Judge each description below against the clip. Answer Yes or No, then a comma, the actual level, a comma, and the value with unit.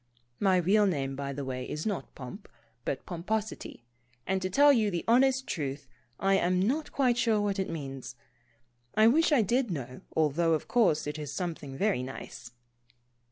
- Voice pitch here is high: No, medium, 180 Hz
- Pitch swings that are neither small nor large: No, wide, 7.4 semitones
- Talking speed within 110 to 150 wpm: No, average, 175 wpm